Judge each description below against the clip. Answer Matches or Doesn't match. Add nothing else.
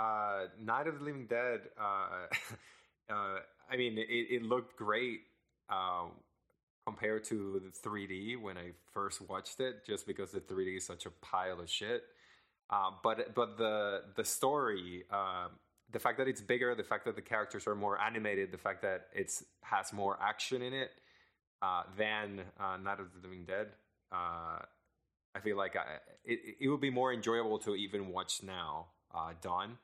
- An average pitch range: Matches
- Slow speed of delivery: Doesn't match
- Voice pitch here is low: Matches